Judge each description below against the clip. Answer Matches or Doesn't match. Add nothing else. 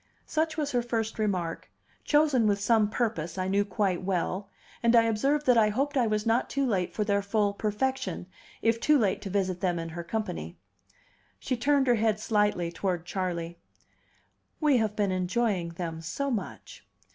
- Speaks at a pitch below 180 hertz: Doesn't match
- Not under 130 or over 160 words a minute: Doesn't match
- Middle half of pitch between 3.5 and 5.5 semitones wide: Matches